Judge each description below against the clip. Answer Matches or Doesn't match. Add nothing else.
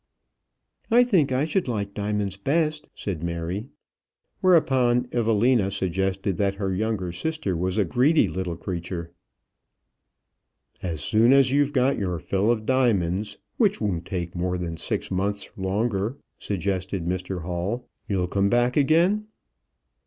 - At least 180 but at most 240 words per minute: Doesn't match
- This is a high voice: Doesn't match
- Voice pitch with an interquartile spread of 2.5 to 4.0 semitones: Doesn't match